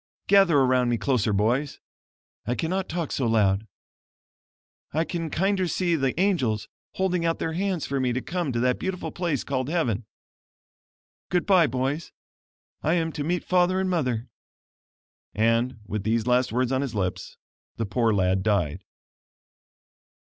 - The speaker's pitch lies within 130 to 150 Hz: Yes, low, 135 Hz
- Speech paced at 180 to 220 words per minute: No, average, 150 wpm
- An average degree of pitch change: No, wide, 7.0 semitones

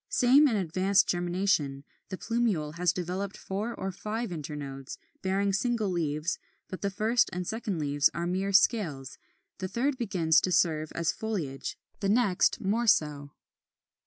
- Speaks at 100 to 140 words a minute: No, average, 150 wpm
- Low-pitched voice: No, medium, 185 Hz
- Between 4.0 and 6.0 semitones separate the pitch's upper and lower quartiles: Yes, average, 5.0 semitones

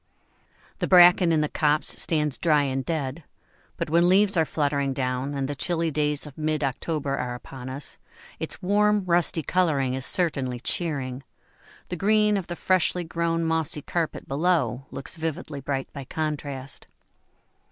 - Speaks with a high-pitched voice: No, medium, 155 Hz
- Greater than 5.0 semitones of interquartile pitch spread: No, average, 3.9 semitones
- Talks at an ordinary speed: Yes, average, 160 wpm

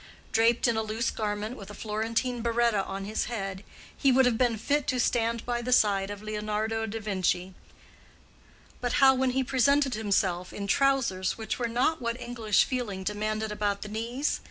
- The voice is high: Yes, high, 225 Hz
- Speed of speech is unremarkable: Yes, average, 180 wpm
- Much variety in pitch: No, average, 2.9 semitones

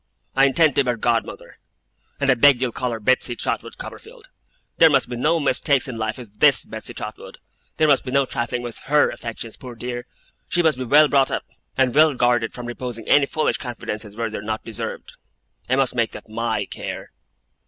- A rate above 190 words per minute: Yes, fast, 205 wpm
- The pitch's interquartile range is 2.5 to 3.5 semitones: Yes, average, 3.1 semitones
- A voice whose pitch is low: Yes, low, 125 Hz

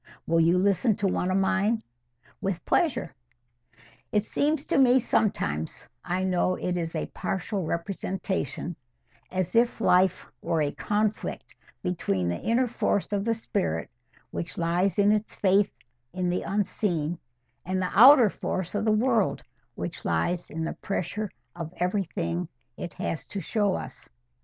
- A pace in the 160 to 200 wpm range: No, average, 140 wpm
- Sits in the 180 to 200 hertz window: Yes, medium, 185 Hz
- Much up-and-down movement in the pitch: No, average, 3.9 semitones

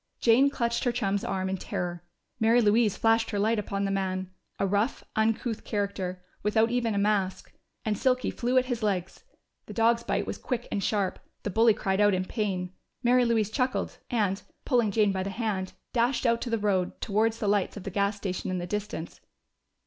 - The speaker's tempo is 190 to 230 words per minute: Yes, average, 200 wpm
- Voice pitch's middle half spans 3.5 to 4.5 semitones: No, average, 3.1 semitones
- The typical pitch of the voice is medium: No, high, 210 Hz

